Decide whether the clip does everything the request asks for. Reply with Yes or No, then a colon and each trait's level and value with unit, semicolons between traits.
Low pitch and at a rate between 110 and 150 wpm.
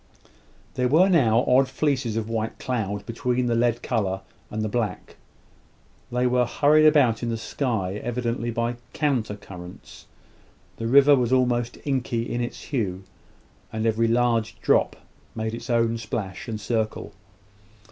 Yes: low, 115 Hz; average, 145 wpm